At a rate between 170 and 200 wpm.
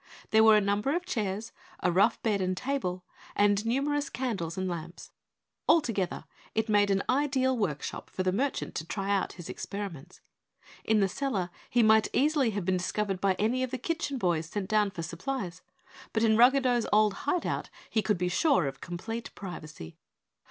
Yes: average, 180 wpm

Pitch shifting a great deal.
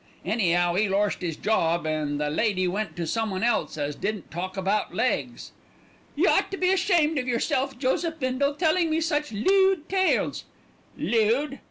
Yes: wide, 8.6 semitones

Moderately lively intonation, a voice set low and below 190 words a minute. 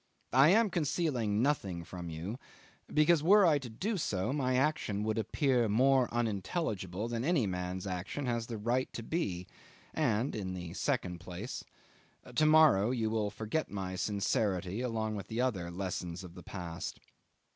No: wide, 6.3 semitones; low, 110 Hz; average, 160 wpm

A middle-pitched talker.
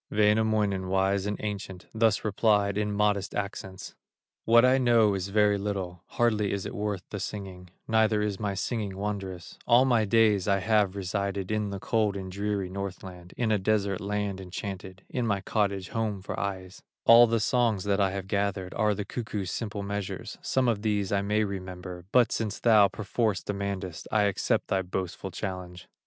No: low, 100 Hz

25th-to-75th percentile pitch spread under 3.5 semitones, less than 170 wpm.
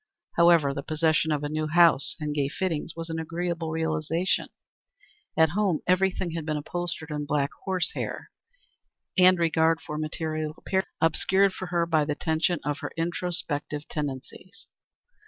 Yes: narrow, 2.5 semitones; average, 160 wpm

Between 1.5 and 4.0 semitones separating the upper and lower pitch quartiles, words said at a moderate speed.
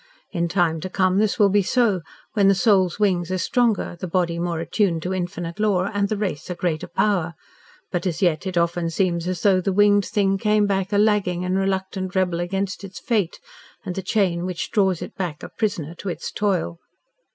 No: narrow, 2.6 semitones; fast, 210 wpm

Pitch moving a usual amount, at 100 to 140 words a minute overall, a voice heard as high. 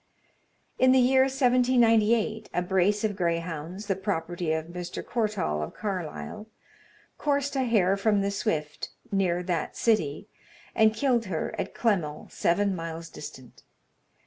Yes: average, 4.9 semitones; slow, 135 wpm; high, 200 Hz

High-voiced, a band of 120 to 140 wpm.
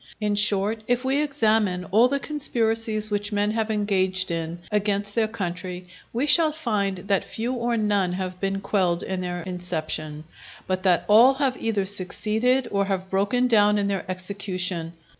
No: high, 205 Hz; average, 165 wpm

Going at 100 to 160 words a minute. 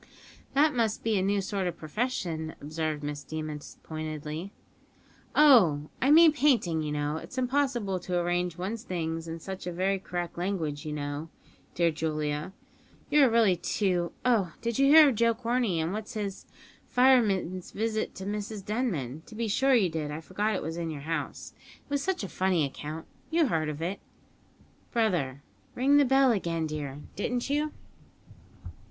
No: average, 170 wpm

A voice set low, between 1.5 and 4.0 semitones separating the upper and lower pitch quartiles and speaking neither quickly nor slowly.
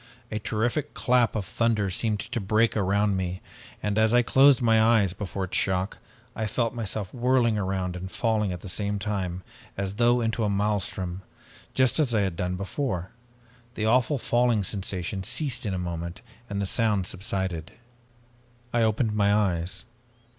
Yes: low, 105 Hz; average, 3.5 semitones; average, 170 wpm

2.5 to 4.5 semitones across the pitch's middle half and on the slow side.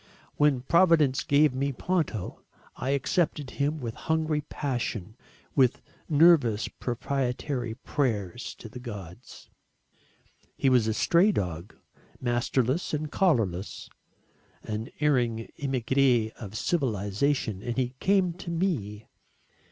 No: average, 5.0 semitones; slow, 110 wpm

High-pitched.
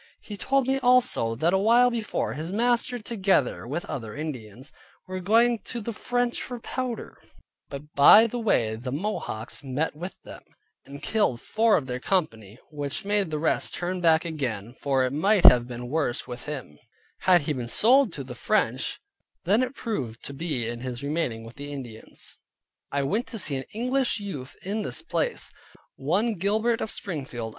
No: medium, 160 Hz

